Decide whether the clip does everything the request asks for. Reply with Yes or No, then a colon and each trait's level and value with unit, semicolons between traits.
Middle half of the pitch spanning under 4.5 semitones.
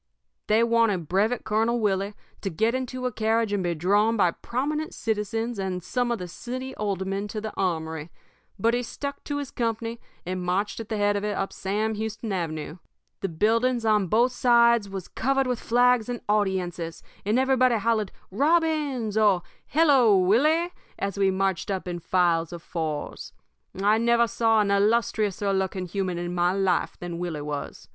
Yes: average, 4.0 semitones